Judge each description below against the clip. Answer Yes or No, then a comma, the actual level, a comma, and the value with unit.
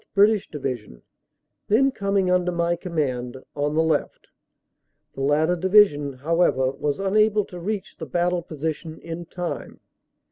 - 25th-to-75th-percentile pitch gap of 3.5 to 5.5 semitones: Yes, average, 4.4 semitones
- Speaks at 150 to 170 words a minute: No, slow, 135 wpm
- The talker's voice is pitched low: No, medium, 170 Hz